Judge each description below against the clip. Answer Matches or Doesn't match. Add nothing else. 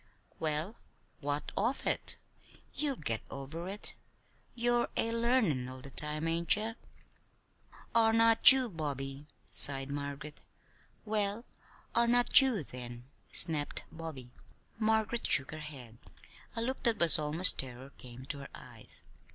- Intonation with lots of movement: Matches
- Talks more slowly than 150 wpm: Matches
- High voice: Doesn't match